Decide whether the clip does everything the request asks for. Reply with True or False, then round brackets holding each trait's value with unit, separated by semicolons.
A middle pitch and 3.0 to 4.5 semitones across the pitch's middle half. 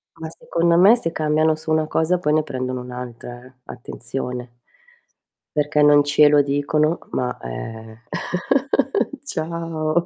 True (150 Hz; 4.1 semitones)